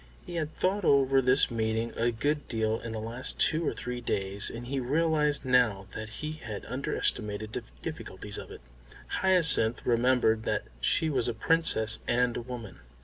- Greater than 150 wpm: Yes, average, 175 wpm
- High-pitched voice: No, low, 125 Hz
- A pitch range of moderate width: Yes, average, 4.6 semitones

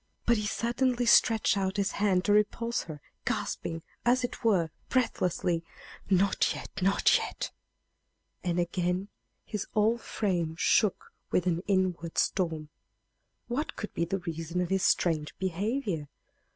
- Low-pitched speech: No, high, 190 Hz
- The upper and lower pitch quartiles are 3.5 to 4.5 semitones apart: Yes, average, 4.0 semitones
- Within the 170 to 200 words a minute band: No, average, 140 wpm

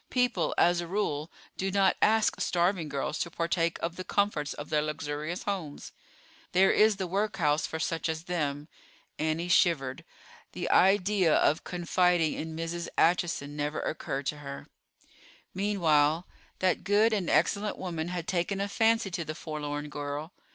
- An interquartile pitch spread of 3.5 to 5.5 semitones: Yes, average, 3.9 semitones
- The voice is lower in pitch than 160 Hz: No, medium, 170 Hz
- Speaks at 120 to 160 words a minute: Yes, average, 155 wpm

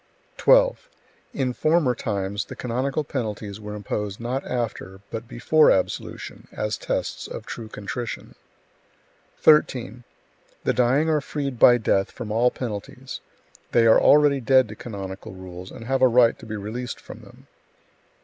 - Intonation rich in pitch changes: No, average, 3.9 semitones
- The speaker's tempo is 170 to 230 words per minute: No, average, 150 wpm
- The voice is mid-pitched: No, low, 120 Hz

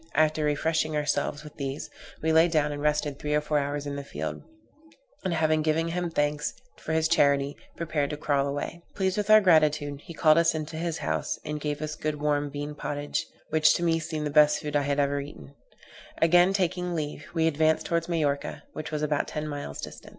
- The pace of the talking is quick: Yes, fast, 210 wpm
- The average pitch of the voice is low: No, medium, 150 Hz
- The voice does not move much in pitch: Yes, narrow, 1.8 semitones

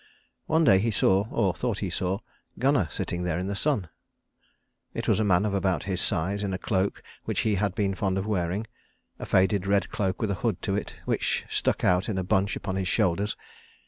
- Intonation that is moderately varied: No, narrow, 2.0 semitones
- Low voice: Yes, low, 100 Hz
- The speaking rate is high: Yes, fast, 215 wpm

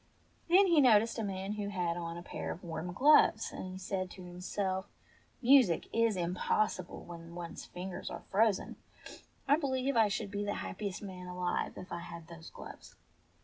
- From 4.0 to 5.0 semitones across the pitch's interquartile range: No, average, 3.6 semitones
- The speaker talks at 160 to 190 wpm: Yes, average, 185 wpm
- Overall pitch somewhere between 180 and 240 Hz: Yes, high, 190 Hz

